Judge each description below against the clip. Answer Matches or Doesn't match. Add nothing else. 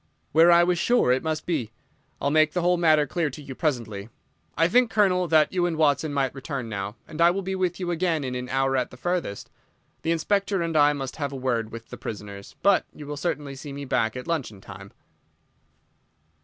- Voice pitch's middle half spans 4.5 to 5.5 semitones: Matches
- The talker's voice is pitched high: Doesn't match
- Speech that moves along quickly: Matches